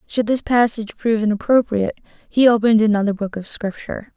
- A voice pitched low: No, high, 220 Hz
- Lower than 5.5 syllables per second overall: No, 6.3 syllables/s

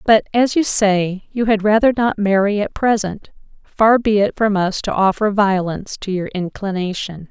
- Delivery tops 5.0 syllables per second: No, 4.6 syllables/s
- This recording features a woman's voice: Yes, female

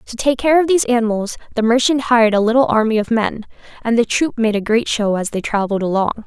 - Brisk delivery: Yes, fast, 240 wpm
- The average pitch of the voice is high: Yes, high, 230 Hz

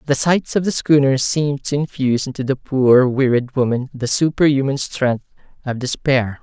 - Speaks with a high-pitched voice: No, low, 135 Hz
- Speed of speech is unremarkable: Yes, average, 170 wpm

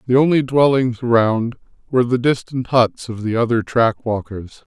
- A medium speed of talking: Yes, average, 165 wpm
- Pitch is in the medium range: No, low, 120 Hz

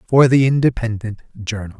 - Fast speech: No, slow, 135 wpm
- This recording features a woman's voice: No, male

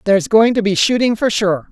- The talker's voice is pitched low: No, high, 210 Hz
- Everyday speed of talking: No, fast, 245 wpm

